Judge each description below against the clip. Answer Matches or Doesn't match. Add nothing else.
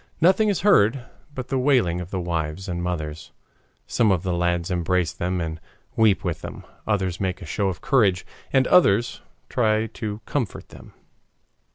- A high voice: Doesn't match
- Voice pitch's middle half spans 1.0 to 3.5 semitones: Doesn't match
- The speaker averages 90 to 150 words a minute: Doesn't match